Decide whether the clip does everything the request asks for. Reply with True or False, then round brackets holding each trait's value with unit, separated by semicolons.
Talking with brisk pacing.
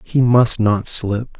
False (170 wpm)